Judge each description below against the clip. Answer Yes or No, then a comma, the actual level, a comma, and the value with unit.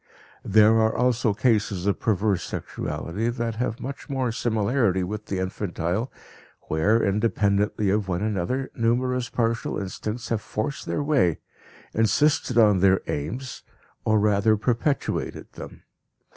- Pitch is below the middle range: Yes, low, 110 Hz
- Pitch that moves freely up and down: No, average, 3.2 semitones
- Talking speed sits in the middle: No, slow, 130 wpm